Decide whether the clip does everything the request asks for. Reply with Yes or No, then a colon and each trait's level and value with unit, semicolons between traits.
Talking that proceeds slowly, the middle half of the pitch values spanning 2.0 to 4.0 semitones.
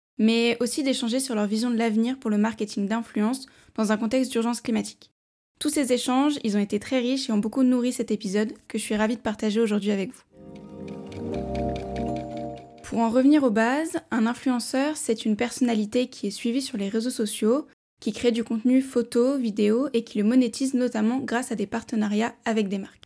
No: average, 195 wpm; narrow, 2.6 semitones